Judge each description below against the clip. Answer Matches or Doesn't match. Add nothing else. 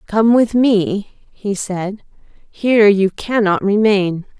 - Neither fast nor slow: Doesn't match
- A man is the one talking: Doesn't match